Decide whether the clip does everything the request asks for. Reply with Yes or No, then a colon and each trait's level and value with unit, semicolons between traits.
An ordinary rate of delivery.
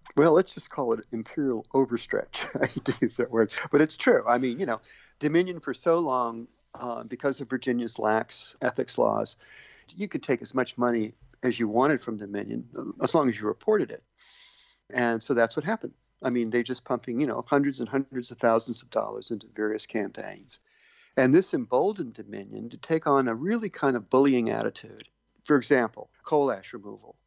Yes: average, 190 wpm